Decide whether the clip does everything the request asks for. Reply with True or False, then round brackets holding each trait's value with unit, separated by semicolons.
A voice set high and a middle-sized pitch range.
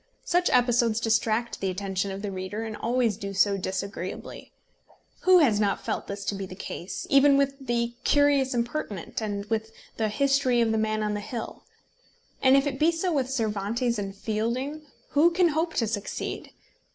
True (225 Hz; 5.0 semitones)